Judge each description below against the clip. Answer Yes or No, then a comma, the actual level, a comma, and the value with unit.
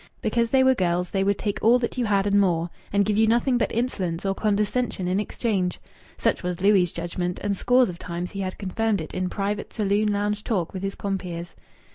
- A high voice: Yes, high, 200 Hz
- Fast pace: Yes, fast, 215 wpm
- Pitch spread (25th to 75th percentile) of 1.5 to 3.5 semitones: Yes, average, 3.1 semitones